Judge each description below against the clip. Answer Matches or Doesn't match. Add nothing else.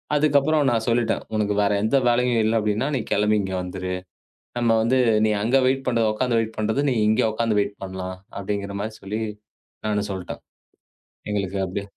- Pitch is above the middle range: Doesn't match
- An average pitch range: Matches